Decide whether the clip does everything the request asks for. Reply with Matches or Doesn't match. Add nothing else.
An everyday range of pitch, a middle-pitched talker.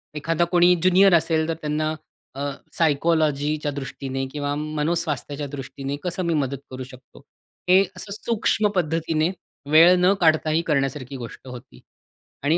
Matches